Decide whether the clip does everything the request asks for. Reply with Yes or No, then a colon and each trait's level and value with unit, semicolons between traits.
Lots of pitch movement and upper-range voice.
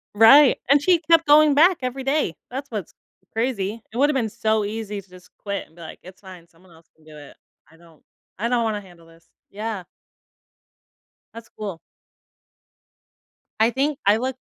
Yes: wide, 6.5 semitones; high, 220 Hz